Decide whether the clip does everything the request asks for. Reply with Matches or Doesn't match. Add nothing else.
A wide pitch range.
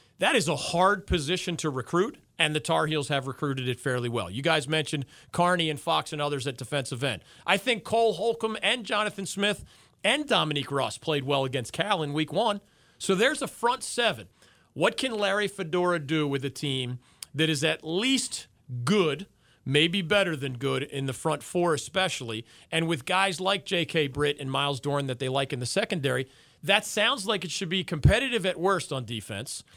Matches